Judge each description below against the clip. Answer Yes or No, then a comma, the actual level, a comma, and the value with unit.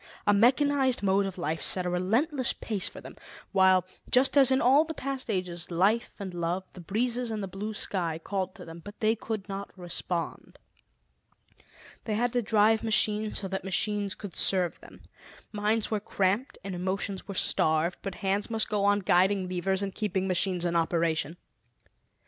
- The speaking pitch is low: No, high, 200 Hz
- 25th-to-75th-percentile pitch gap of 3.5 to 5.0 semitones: No, average, 3.1 semitones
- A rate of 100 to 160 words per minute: No, average, 180 wpm